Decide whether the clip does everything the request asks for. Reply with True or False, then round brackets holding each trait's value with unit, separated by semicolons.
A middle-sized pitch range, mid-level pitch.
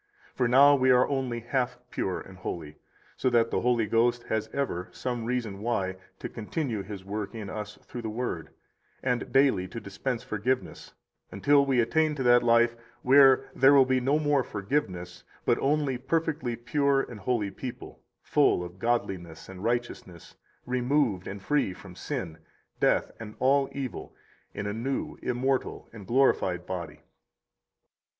False (4.7 semitones; 120 Hz)